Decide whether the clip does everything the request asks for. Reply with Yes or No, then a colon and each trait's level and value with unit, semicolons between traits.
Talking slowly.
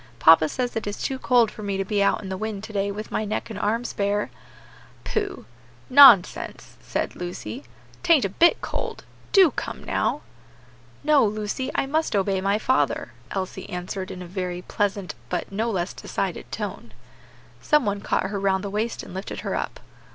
No: average, 185 wpm